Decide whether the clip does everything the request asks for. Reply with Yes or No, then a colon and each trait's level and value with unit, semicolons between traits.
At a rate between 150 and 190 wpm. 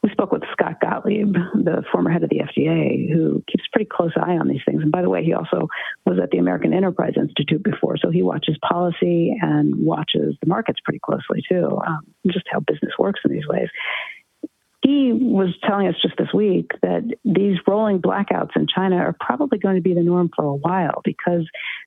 No: fast, 205 wpm